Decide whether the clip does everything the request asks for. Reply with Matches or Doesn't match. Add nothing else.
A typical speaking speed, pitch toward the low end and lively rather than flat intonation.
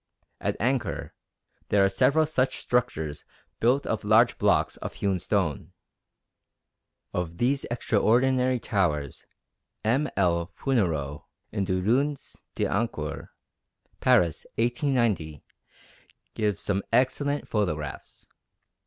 Doesn't match